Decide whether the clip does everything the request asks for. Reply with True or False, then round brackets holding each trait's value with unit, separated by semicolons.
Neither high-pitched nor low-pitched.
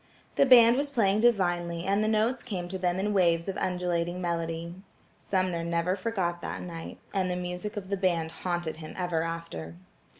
True (180 Hz)